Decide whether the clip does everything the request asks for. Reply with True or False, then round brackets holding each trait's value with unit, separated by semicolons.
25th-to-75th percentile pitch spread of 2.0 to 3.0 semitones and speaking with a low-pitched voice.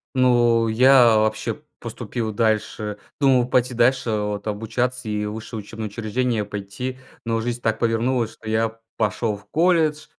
True (2.6 semitones; 115 Hz)